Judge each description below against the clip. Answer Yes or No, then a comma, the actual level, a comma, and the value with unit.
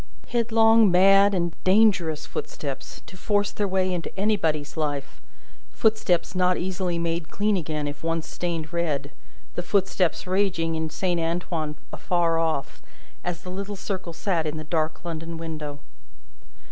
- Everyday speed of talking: Yes, average, 145 wpm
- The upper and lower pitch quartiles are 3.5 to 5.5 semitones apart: No, average, 3.1 semitones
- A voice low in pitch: No, medium, 175 Hz